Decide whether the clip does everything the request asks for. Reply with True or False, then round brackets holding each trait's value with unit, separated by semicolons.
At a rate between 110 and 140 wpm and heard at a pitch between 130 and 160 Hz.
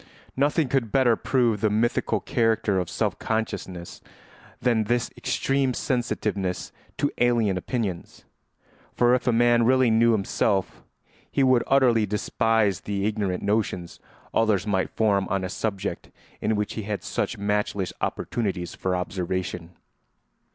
False (135 wpm; 110 Hz)